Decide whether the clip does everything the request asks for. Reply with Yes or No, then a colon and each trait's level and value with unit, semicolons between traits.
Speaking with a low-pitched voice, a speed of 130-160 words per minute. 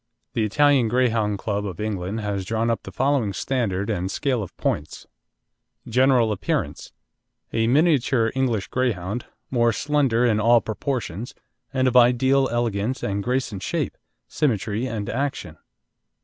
Yes: low, 115 Hz; average, 140 wpm